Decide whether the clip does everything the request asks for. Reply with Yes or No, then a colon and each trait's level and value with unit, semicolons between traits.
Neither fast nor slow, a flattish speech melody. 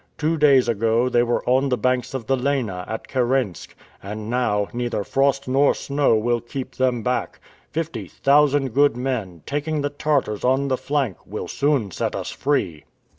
No: average, 175 wpm; average, 3.5 semitones